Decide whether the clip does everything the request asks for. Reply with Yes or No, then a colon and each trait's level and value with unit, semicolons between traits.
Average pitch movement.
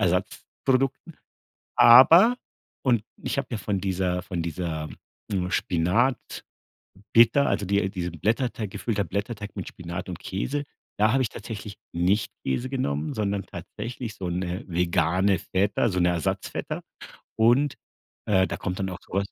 Yes: average, 4.6 semitones